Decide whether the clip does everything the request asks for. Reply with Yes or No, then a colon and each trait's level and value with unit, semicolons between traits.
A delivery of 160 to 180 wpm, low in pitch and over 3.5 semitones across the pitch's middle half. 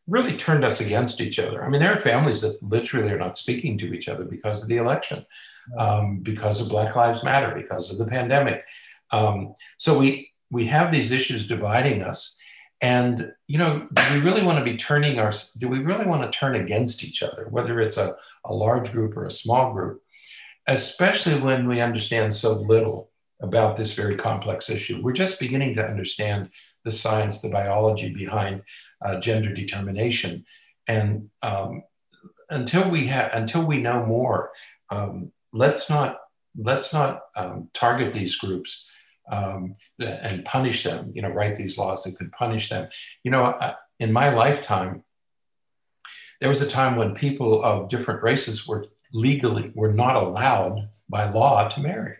Yes: average, 170 wpm; low, 115 Hz; average, 4.3 semitones